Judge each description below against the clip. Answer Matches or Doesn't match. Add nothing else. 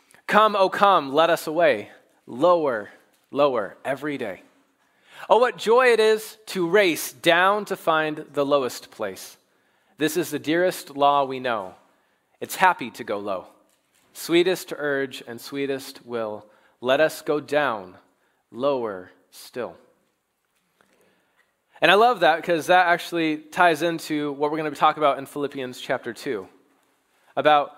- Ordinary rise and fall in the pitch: Matches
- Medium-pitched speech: Matches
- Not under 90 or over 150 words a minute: Matches